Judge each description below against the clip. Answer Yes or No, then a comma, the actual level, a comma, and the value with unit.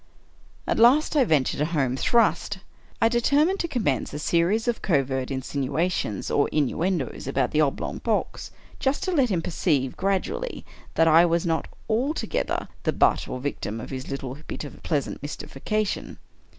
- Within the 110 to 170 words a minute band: Yes, average, 165 wpm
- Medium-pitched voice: Yes, medium, 165 Hz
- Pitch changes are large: Yes, wide, 8.6 semitones